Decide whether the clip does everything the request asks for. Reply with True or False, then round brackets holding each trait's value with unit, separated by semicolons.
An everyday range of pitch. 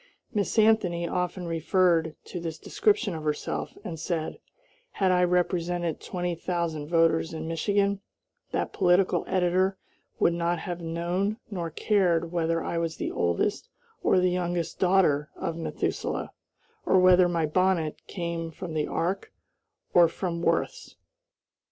False (1.9 semitones)